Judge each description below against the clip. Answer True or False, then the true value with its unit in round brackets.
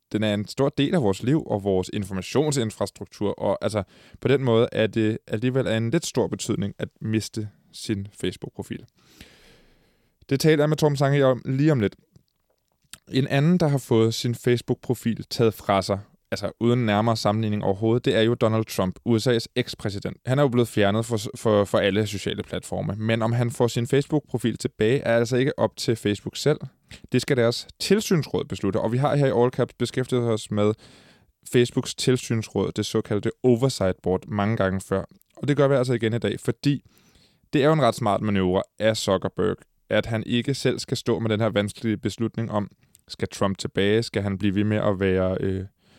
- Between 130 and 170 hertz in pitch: False (115 Hz)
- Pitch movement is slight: False (3.6 semitones)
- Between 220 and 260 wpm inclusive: False (195 wpm)